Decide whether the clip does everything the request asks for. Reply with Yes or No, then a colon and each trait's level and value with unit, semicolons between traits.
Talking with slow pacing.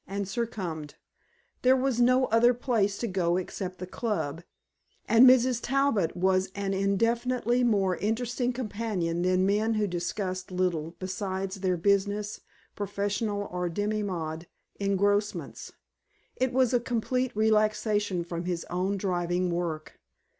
Yes: slow, 130 wpm